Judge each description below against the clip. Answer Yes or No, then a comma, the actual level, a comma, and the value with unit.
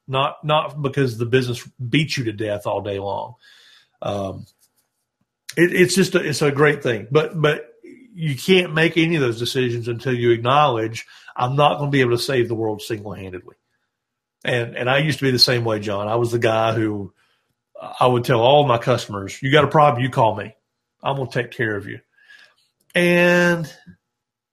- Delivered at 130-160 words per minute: No, average, 195 wpm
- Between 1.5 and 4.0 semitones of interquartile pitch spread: No, average, 4.8 semitones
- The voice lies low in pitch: Yes, low, 130 Hz